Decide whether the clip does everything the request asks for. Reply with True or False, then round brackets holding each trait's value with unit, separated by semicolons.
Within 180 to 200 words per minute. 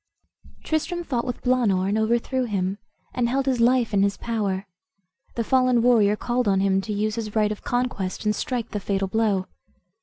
True (185 wpm)